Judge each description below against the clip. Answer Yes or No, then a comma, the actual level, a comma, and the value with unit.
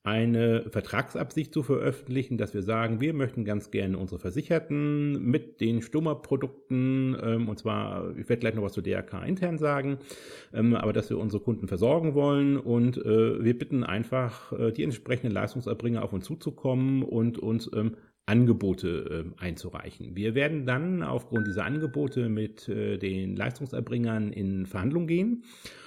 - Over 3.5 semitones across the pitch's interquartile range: Yes, average, 4.5 semitones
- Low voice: Yes, low, 115 Hz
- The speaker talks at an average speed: Yes, average, 140 wpm